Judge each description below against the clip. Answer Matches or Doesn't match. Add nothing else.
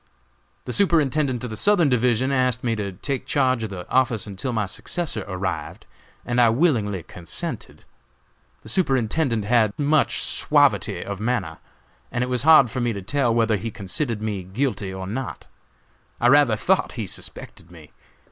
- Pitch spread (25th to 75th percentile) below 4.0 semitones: Doesn't match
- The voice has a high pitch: Doesn't match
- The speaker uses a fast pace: Doesn't match